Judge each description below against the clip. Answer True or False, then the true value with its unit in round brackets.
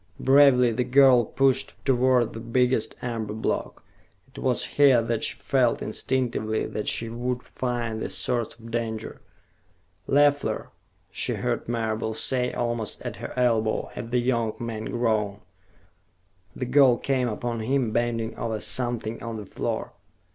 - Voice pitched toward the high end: False (120 Hz)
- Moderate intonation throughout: False (2.1 semitones)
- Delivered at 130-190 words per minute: True (145 wpm)